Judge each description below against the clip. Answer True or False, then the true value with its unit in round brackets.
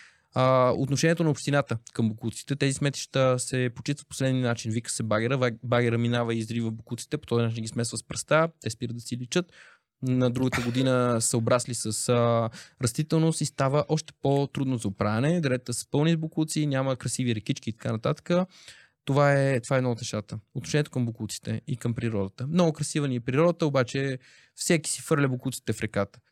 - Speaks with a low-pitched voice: True (130 Hz)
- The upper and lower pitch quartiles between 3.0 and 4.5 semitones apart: True (3.4 semitones)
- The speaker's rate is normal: False (180 wpm)